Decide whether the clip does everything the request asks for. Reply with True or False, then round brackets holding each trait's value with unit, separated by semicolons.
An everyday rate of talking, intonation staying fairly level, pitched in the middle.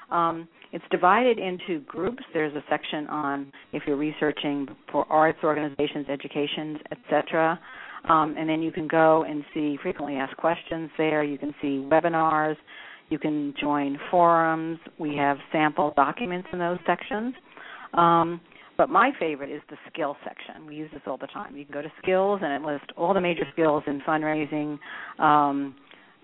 True (170 wpm; 2.3 semitones; 155 Hz)